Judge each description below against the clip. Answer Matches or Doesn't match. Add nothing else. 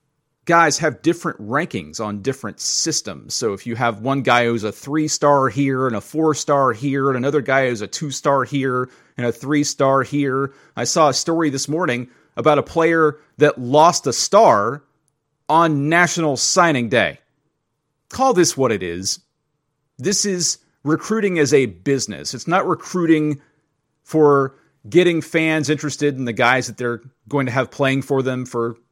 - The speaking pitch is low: Doesn't match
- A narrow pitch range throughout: Doesn't match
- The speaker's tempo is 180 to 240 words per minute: Doesn't match